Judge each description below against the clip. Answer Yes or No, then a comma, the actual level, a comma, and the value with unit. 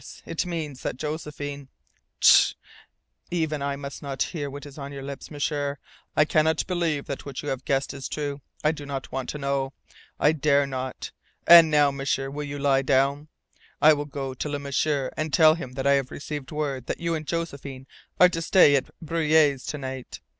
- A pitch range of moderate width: No, narrow, 1.9 semitones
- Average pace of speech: Yes, average, 190 wpm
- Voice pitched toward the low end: No, medium, 145 Hz